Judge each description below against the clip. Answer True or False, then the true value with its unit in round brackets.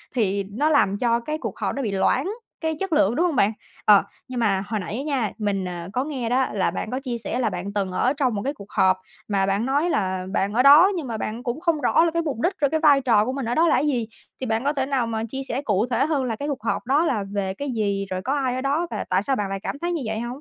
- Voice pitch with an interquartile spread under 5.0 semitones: False (5.6 semitones)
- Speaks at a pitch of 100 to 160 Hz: False (245 Hz)